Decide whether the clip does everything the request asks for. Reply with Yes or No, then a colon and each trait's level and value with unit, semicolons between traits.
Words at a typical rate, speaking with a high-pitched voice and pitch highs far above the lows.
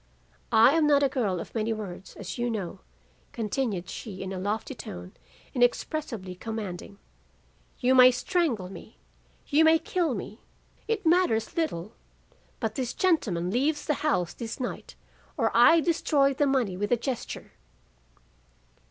Yes: average, 145 wpm; high, 240 Hz; wide, 6.5 semitones